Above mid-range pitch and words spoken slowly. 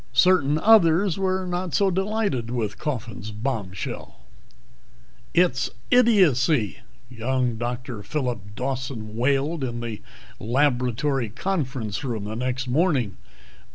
No: low, 130 Hz; slow, 105 wpm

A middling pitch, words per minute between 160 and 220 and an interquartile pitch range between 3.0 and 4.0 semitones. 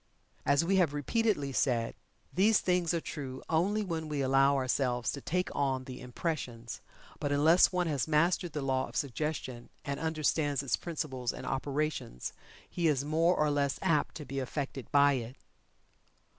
Yes: medium, 145 Hz; average, 165 wpm; average, 3.5 semitones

